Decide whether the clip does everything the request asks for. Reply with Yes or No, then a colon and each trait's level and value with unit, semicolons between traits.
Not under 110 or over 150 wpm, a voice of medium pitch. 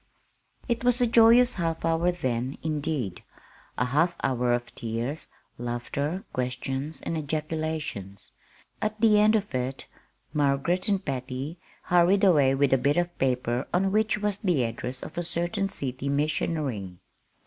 Yes: average, 145 wpm; medium, 150 Hz